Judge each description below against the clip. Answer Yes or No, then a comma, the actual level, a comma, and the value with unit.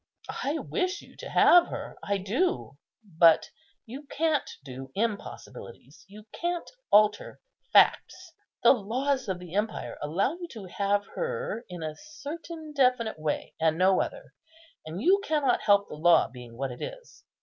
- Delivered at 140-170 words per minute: Yes, average, 150 wpm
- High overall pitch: Yes, high, 215 Hz